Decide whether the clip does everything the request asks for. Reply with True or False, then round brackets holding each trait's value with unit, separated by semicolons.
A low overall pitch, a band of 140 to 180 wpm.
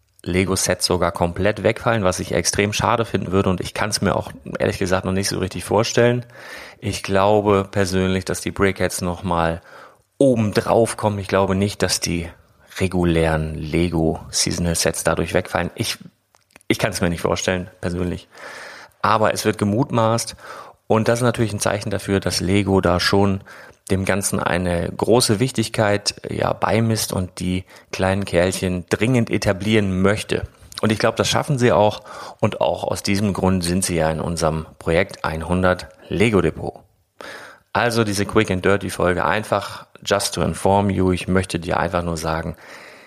True (95 Hz; 165 wpm)